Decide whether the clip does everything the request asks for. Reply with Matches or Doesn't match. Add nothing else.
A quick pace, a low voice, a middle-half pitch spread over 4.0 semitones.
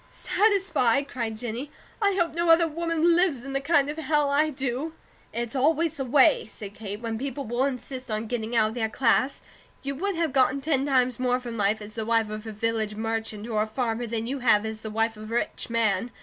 Doesn't match